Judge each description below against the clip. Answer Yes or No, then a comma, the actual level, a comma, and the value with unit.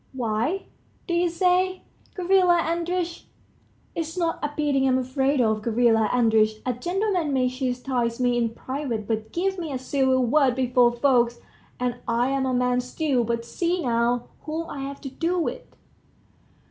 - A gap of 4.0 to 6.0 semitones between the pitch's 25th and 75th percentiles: Yes, wide, 5.5 semitones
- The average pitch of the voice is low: No, very high, 260 Hz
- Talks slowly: No, average, 155 wpm